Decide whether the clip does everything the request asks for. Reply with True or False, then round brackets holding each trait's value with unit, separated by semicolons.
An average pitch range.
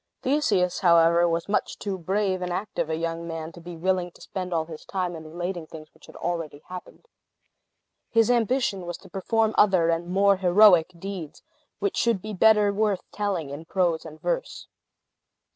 True (3.3 semitones)